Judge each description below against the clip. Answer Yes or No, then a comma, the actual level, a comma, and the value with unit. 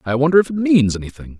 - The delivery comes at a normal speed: No, fast, 260 wpm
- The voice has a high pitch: No, medium, 140 Hz